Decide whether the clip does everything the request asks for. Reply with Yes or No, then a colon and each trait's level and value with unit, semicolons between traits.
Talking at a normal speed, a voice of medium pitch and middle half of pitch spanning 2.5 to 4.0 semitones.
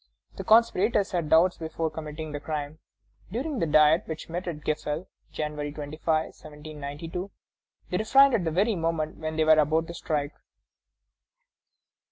Yes: average, 150 wpm; medium, 160 Hz; average, 2.8 semitones